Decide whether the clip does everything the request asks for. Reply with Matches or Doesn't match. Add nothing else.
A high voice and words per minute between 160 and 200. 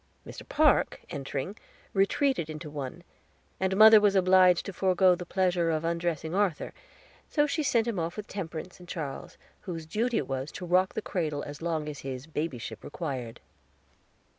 Doesn't match